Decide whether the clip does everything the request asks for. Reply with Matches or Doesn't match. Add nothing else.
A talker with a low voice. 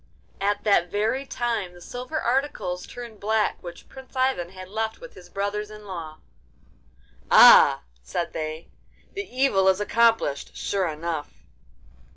Doesn't match